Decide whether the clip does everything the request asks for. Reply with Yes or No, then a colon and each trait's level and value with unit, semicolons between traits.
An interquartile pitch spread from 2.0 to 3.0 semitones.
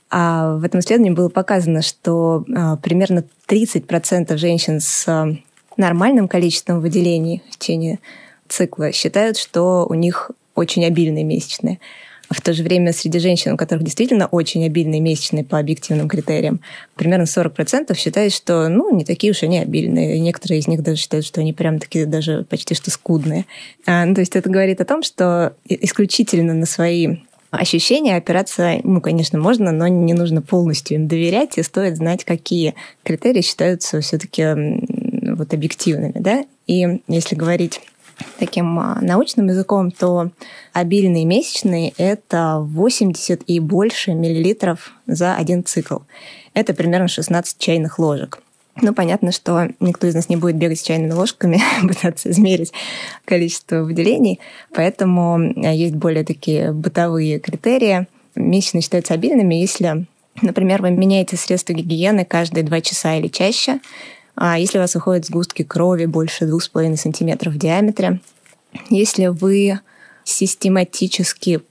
Yes: narrow, 2.6 semitones